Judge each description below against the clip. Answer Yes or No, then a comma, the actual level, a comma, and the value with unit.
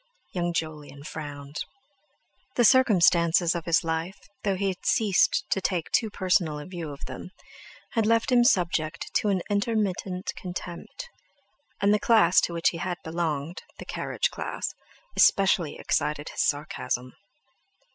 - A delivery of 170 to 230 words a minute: No, slow, 135 wpm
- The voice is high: No, medium, 175 Hz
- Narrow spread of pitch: No, average, 3.9 semitones